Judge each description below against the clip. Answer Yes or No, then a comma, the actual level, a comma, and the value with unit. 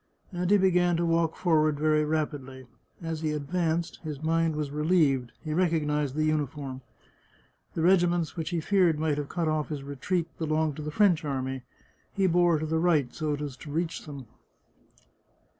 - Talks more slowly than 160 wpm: No, average, 185 wpm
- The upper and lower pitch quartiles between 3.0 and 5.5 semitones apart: No, narrow, 2.4 semitones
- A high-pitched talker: No, medium, 155 Hz